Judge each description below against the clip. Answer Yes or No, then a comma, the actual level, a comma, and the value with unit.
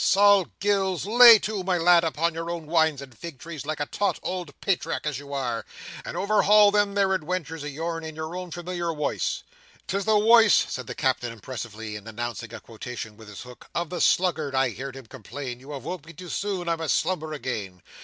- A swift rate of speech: Yes, fast, 215 wpm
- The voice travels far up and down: Yes, wide, 5.8 semitones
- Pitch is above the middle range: No, medium, 160 Hz